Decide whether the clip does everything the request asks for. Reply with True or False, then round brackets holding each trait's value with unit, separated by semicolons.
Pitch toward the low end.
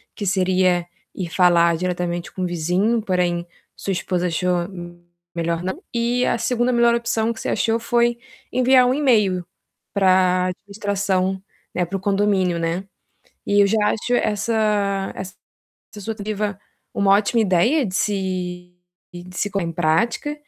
False (195 Hz)